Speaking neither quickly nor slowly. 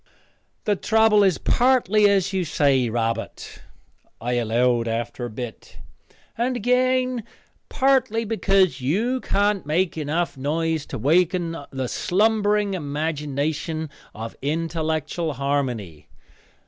No: slow, 110 wpm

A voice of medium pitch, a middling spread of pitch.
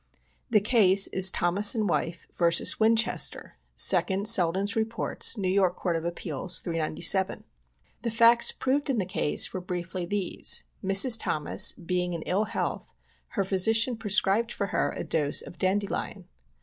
No: high, 195 Hz; average, 3.7 semitones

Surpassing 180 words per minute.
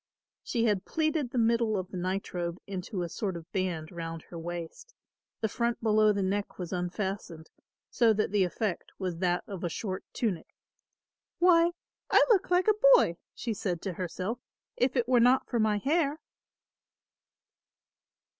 No: average, 165 wpm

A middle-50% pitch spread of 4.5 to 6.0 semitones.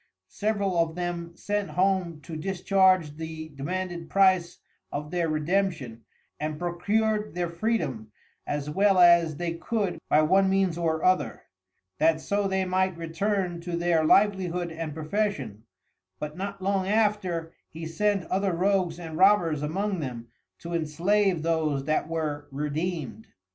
No: average, 3.5 semitones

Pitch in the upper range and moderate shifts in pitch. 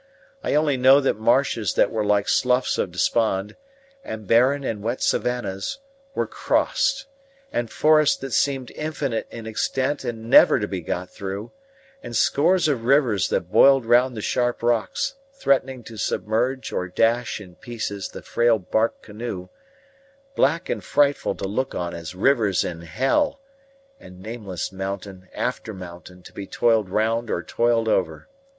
No: low, 115 Hz; average, 4.9 semitones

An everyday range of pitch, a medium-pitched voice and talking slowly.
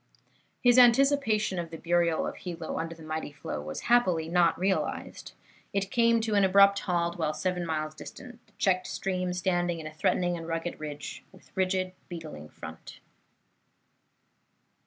No: average, 3.3 semitones; medium, 175 Hz; average, 155 wpm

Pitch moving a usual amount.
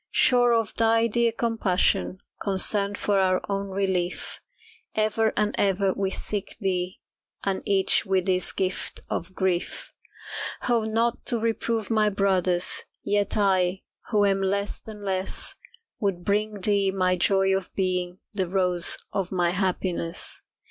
No: narrow, 2.3 semitones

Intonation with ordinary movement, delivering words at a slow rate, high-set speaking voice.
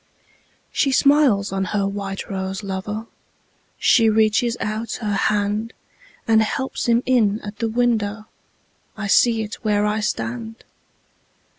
No: narrow, 2.2 semitones; slow, 115 wpm; high, 215 Hz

